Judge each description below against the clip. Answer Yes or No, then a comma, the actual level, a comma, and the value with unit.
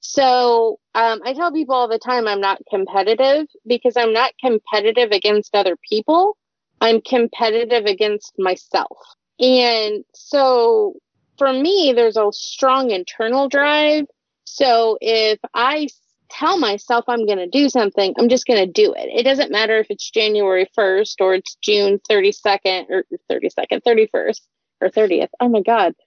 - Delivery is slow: No, average, 145 wpm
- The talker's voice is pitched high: Yes, high, 230 Hz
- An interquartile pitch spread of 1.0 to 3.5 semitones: No, average, 4.2 semitones